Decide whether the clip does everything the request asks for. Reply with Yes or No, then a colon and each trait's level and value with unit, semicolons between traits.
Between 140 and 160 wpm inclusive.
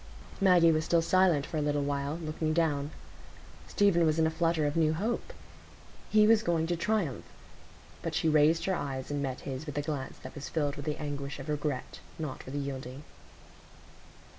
No: average, 190 wpm